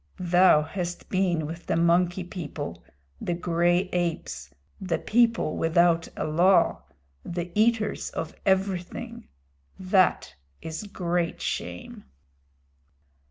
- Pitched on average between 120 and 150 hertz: No, medium, 175 Hz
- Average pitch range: No, narrow, 2.1 semitones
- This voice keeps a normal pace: No, slow, 105 wpm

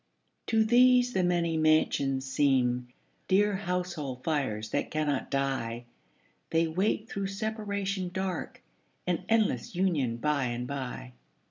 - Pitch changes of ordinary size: No, wide, 6.6 semitones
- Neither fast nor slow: No, slow, 120 wpm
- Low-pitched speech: No, medium, 160 Hz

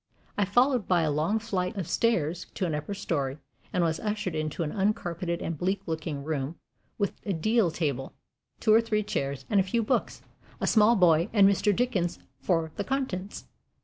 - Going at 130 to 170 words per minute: No, average, 185 wpm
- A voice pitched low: No, medium, 185 Hz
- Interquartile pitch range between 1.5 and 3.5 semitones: No, average, 4.8 semitones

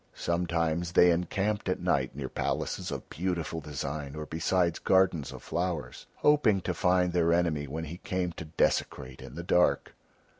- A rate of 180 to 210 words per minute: No, average, 160 wpm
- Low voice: Yes, very low, 85 Hz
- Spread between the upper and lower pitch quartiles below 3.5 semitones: Yes, average, 2.7 semitones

